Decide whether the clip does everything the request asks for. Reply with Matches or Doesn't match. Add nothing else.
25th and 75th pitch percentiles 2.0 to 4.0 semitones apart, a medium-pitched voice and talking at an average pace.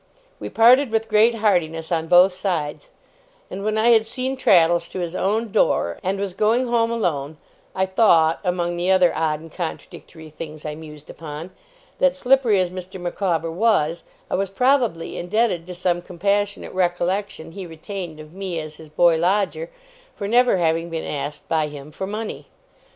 Doesn't match